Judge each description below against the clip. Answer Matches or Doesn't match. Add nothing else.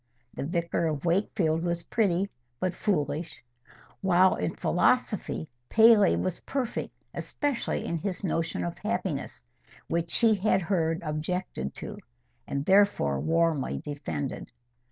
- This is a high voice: Doesn't match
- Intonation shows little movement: Doesn't match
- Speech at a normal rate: Doesn't match